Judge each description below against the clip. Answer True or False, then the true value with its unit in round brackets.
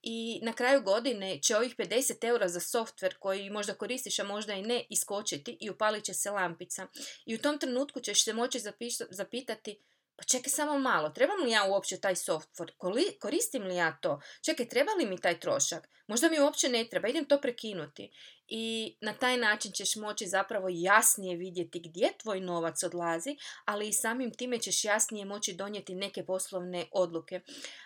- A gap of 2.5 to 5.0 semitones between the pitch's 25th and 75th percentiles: True (4.4 semitones)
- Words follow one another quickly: True (180 wpm)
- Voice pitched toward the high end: True (210 Hz)